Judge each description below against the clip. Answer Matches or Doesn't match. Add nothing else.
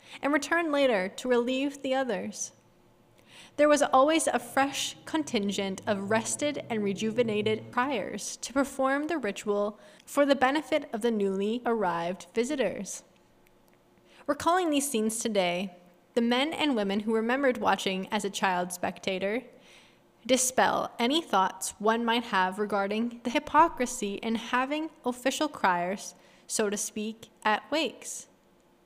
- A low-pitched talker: Doesn't match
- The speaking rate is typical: Doesn't match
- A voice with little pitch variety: Doesn't match